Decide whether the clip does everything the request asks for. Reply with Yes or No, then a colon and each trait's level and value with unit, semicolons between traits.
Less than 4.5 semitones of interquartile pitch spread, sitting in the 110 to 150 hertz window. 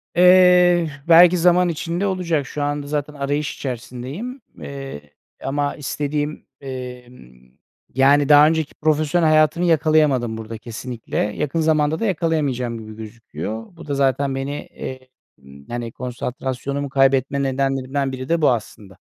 Yes: average, 3.9 semitones; medium, 140 Hz